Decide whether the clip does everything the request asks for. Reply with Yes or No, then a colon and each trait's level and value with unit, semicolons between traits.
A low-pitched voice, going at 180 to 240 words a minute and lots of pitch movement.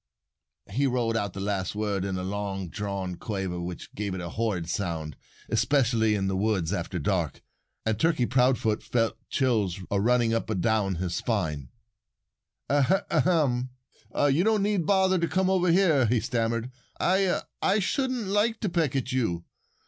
No: low, 115 Hz; average, 165 wpm; wide, 7.1 semitones